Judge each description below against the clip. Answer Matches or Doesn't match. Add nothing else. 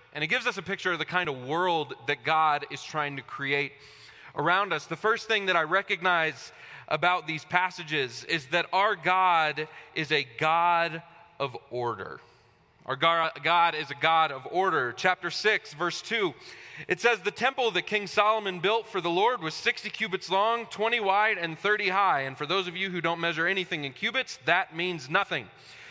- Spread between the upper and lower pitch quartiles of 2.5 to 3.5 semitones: Doesn't match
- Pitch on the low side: Doesn't match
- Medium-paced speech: Matches